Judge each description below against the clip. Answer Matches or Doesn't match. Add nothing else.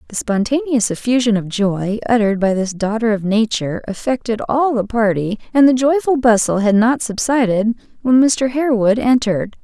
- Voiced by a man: Doesn't match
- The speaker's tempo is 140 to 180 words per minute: Matches